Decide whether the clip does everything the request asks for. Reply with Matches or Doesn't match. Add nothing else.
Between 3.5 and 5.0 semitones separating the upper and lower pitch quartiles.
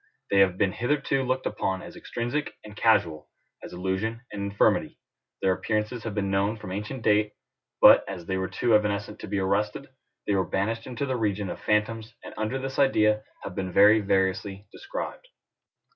Doesn't match